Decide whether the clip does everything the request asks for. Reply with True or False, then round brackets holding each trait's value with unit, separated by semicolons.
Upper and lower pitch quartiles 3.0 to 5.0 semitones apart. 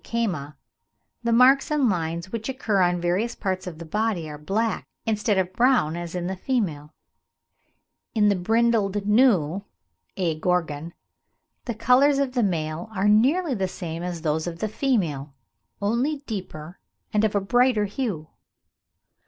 False (5.5 semitones)